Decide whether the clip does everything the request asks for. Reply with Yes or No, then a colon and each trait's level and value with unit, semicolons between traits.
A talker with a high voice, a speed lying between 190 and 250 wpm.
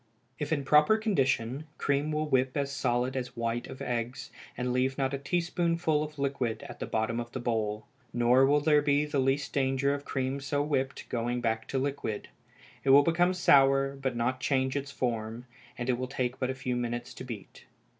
No: low, 135 Hz; average, 200 wpm